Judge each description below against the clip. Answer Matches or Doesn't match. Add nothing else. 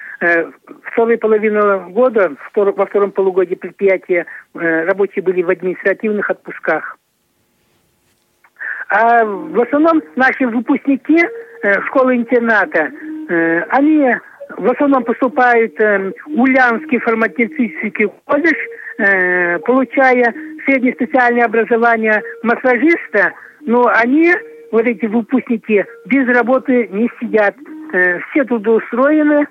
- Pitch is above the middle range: Matches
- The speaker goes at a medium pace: Doesn't match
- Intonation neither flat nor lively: Matches